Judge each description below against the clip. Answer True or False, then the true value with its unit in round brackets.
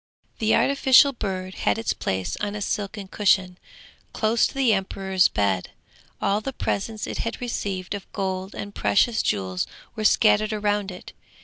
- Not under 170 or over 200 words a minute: False (155 wpm)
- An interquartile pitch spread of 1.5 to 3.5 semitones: True (2.6 semitones)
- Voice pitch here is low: False (200 Hz)